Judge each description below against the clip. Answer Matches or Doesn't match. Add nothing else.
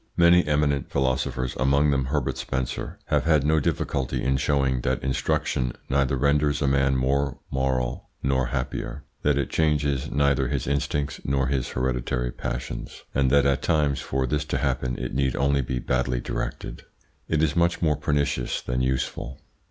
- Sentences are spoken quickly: Doesn't match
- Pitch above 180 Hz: Doesn't match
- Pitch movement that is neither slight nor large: Doesn't match